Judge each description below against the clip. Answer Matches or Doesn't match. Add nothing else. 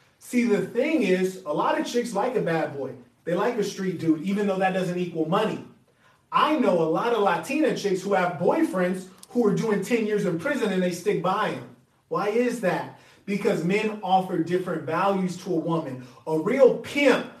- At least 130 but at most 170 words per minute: Doesn't match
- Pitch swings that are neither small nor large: Matches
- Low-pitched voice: Doesn't match